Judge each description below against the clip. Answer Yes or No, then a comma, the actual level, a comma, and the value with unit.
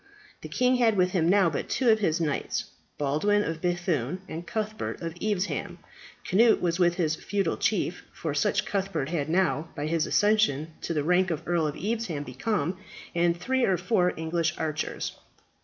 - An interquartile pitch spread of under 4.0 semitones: No, average, 4.3 semitones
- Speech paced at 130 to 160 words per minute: No, average, 175 wpm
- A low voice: No, medium, 175 Hz